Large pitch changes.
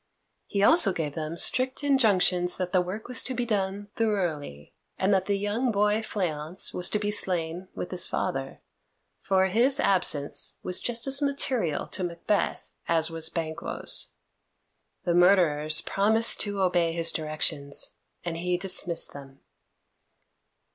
No: average, 4.1 semitones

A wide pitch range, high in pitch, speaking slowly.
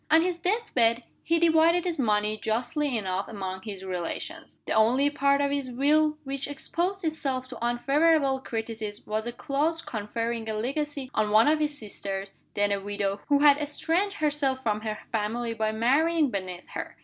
No: wide, 5.7 semitones; very high, 255 Hz; average, 175 wpm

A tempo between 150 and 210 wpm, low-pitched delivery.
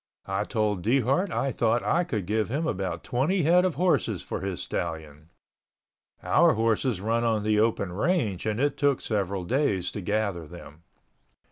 Yes: average, 165 wpm; low, 110 Hz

